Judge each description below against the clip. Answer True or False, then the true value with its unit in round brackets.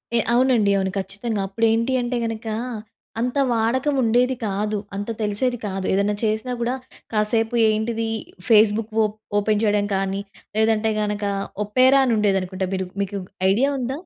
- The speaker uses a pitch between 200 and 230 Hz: True (220 Hz)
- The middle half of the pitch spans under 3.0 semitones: True (2.6 semitones)